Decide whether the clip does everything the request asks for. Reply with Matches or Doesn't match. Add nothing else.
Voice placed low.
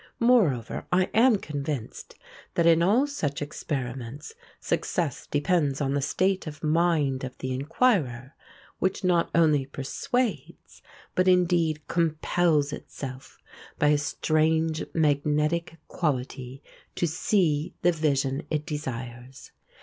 Doesn't match